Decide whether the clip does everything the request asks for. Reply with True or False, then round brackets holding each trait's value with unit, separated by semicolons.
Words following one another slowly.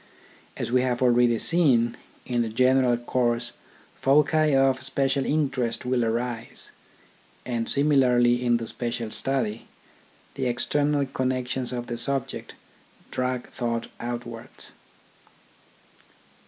True (110 wpm)